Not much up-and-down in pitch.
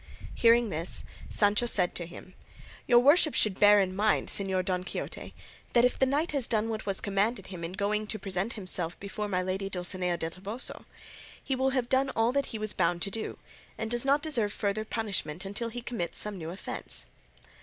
No: average, 4.2 semitones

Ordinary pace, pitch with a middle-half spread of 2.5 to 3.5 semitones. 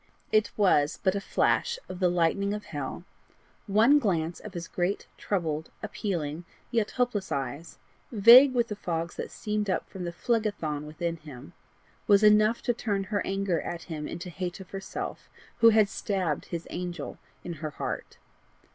No: average, 165 wpm; average, 4.1 semitones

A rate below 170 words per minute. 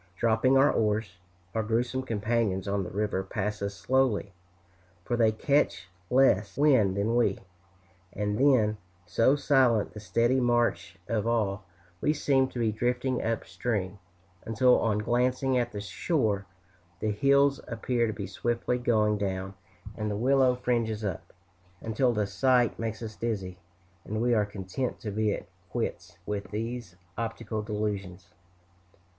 Yes: average, 150 wpm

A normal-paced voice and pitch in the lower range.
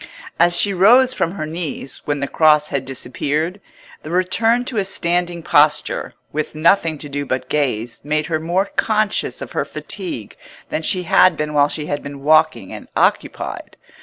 No: average, 175 wpm; medium, 155 Hz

